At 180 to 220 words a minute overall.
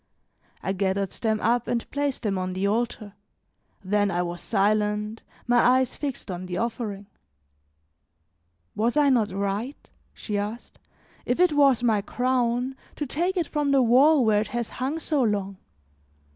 No: average, 160 wpm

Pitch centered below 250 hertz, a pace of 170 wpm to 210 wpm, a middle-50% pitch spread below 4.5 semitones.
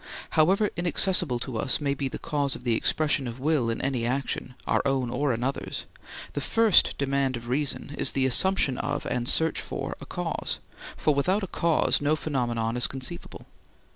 Yes: medium, 140 Hz; average, 180 wpm; average, 3.6 semitones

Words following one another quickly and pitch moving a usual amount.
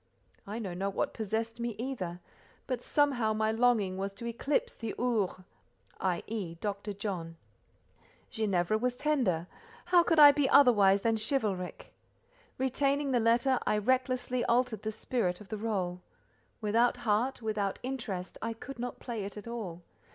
No: average, 150 wpm; average, 4.0 semitones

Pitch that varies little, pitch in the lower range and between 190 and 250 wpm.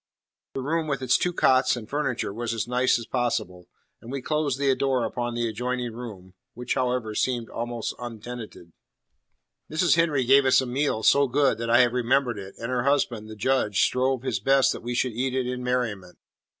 Yes: narrow, 2.3 semitones; low, 125 Hz; average, 200 wpm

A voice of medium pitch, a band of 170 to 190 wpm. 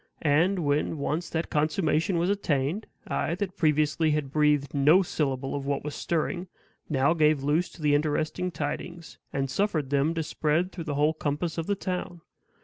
Yes: medium, 155 Hz; average, 175 wpm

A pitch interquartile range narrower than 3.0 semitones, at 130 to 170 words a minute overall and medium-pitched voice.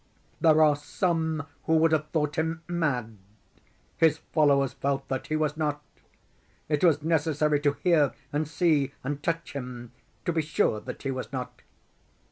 Yes: narrow, 2.4 semitones; average, 160 wpm; medium, 150 Hz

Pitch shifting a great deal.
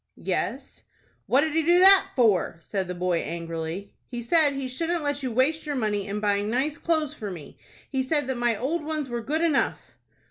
Yes: wide, 7.0 semitones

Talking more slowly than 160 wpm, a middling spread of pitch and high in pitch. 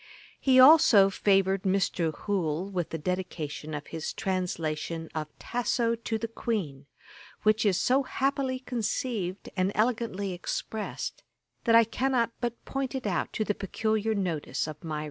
Yes: average, 150 wpm; average, 5.0 semitones; high, 200 Hz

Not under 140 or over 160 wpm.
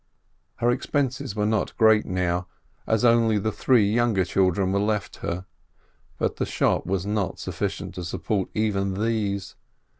Yes: average, 150 wpm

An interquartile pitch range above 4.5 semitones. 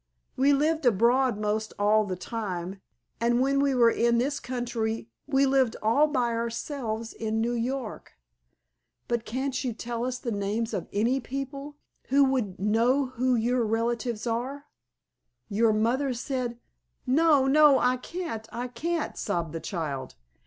No: average, 3.3 semitones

